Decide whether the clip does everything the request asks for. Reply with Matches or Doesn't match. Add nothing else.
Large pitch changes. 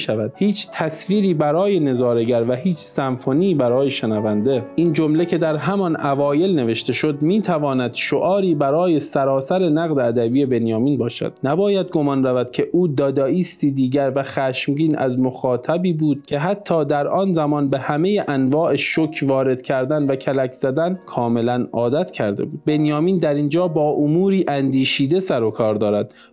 Doesn't match